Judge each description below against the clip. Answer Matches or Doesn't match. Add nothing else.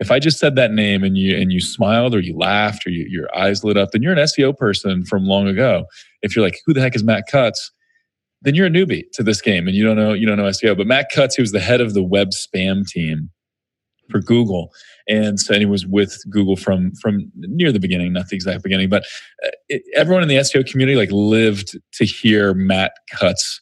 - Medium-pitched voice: Doesn't match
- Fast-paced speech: Matches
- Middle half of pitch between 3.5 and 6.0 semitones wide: Matches